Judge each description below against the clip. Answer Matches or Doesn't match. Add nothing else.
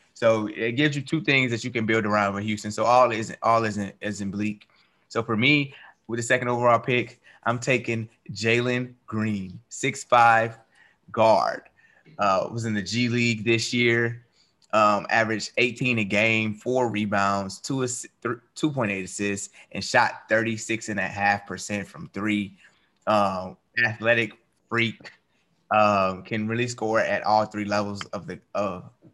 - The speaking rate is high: Doesn't match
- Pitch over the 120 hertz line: Doesn't match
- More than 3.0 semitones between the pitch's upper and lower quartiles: Doesn't match